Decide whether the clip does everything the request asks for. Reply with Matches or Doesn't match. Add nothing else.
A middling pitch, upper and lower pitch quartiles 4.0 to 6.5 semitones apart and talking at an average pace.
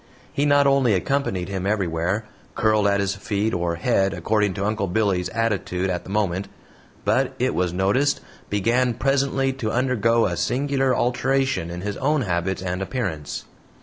Doesn't match